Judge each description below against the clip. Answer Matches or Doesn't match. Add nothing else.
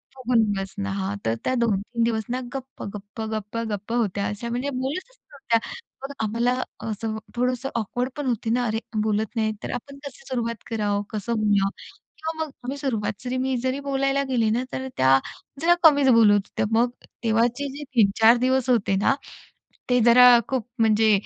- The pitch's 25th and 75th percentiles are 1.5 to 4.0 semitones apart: Matches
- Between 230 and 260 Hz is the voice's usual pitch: Matches